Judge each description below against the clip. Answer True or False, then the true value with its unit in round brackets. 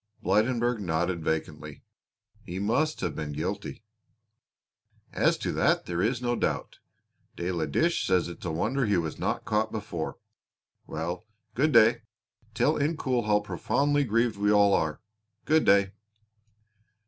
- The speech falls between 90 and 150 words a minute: True (145 wpm)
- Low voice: True (105 Hz)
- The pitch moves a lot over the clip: True (5.7 semitones)